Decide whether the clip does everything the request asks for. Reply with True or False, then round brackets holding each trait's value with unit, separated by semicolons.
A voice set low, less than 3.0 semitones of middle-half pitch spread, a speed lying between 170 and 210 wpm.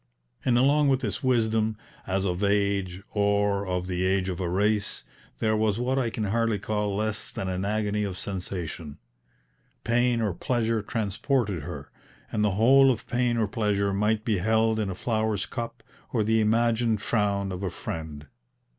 True (105 Hz; 2.6 semitones; 175 wpm)